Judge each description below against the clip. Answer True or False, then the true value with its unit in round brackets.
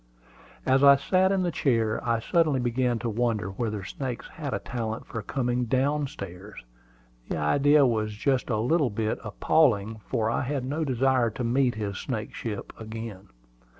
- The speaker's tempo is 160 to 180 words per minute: True (165 wpm)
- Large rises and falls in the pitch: False (3.8 semitones)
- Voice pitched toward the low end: True (120 Hz)